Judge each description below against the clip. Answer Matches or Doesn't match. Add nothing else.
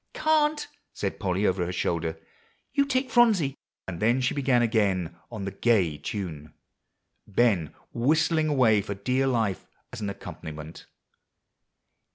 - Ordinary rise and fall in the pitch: Doesn't match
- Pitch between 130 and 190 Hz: Doesn't match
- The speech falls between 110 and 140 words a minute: Matches